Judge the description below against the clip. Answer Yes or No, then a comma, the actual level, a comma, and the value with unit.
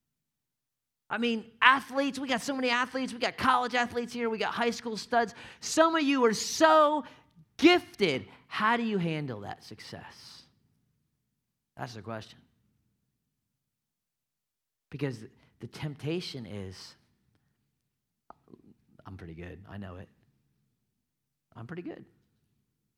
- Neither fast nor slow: No, slow, 120 wpm